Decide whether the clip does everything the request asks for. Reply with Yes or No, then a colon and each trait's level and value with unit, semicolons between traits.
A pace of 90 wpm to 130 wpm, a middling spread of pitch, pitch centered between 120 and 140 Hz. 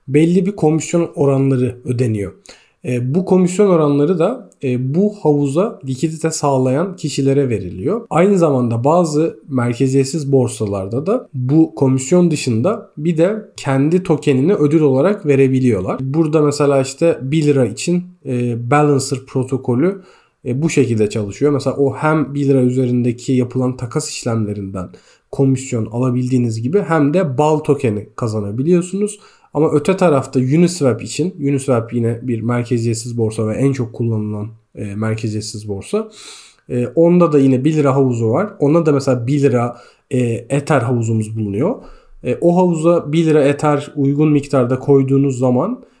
No: fast, 140 wpm; average, 4.2 semitones; low, 135 Hz